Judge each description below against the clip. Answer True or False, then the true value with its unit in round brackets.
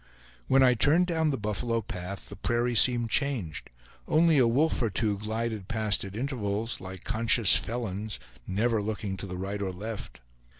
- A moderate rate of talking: True (170 wpm)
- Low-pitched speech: True (110 Hz)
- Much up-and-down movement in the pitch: False (3.4 semitones)